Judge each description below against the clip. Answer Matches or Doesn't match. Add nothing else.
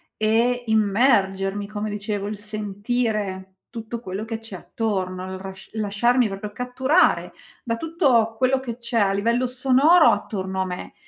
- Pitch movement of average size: Matches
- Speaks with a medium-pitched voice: Doesn't match